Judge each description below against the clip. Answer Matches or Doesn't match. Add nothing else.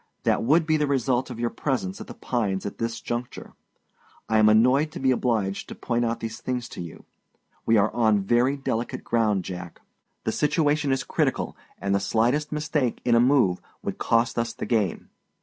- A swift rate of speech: Doesn't match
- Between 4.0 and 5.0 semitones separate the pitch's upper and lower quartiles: Doesn't match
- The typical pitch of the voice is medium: Doesn't match